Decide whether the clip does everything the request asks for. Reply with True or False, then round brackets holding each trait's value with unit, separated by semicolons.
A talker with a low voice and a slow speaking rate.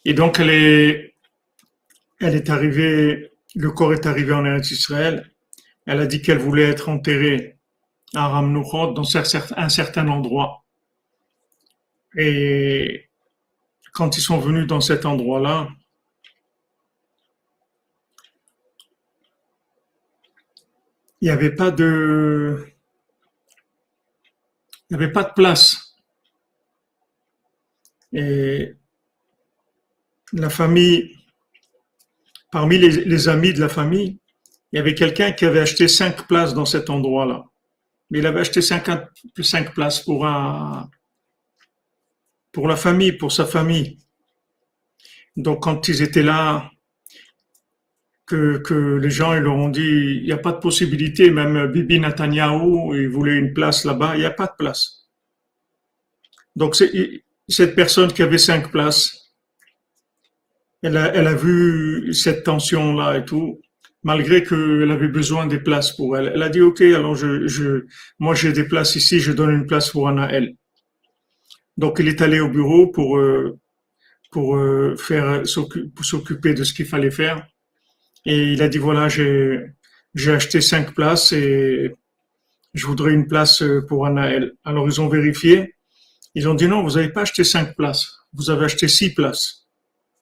False (155 Hz; 140 wpm)